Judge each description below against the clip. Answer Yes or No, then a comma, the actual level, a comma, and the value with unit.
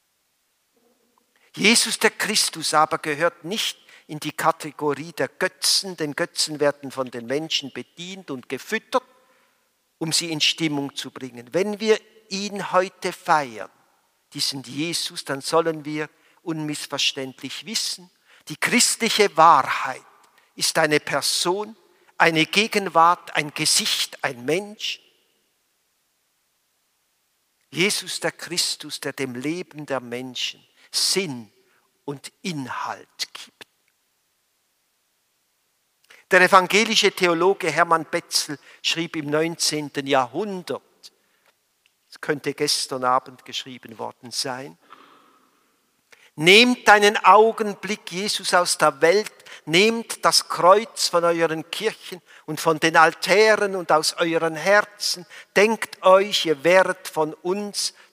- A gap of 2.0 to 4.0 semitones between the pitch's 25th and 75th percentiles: No, average, 4.6 semitones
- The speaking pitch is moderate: Yes, medium, 165 Hz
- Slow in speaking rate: Yes, slow, 110 wpm